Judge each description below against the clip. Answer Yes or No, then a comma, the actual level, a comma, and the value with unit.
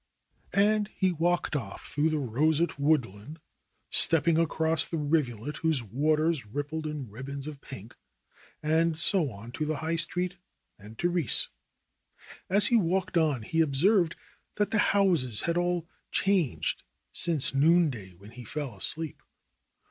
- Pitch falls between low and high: Yes, medium, 155 Hz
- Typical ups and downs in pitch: Yes, average, 4.1 semitones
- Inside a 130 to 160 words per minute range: Yes, average, 140 wpm